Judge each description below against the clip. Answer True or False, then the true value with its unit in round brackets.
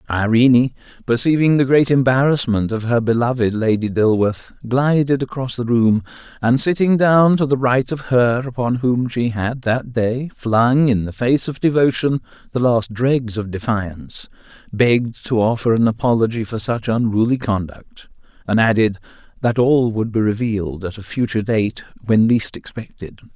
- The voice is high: False (120 Hz)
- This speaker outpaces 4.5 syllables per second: True (4.7 syllables/s)